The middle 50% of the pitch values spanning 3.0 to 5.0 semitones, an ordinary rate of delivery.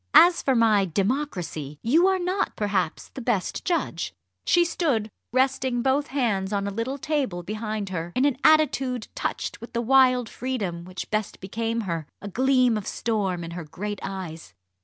No: wide, 5.6 semitones; average, 170 wpm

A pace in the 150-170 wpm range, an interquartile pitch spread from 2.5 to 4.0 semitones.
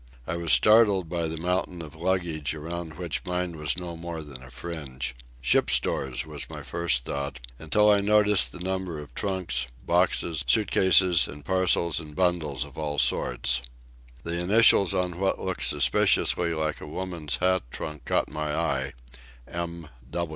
Yes: average, 160 wpm; average, 3.6 semitones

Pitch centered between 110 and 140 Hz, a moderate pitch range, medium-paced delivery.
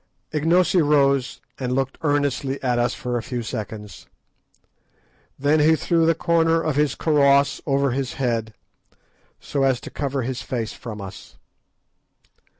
Yes: low, 135 Hz; average, 3.5 semitones; average, 145 wpm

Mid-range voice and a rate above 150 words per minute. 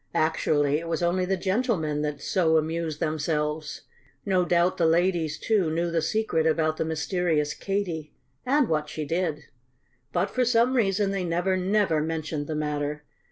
Yes: medium, 165 Hz; average, 160 wpm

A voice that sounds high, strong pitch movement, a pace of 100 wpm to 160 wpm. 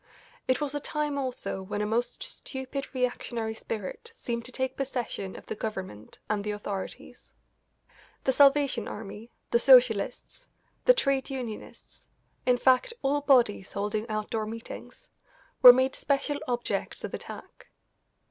No: high, 245 Hz; average, 4.2 semitones; average, 140 wpm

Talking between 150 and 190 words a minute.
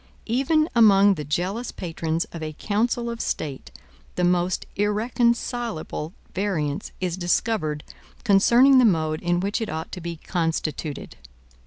No: slow, 135 wpm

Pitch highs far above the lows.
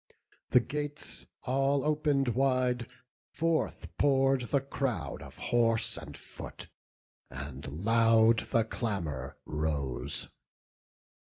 Yes: wide, 7.7 semitones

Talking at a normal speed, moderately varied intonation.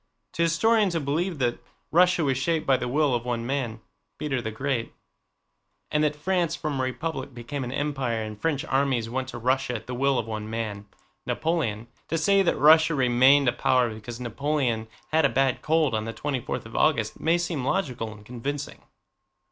Yes: average, 180 wpm; average, 4.5 semitones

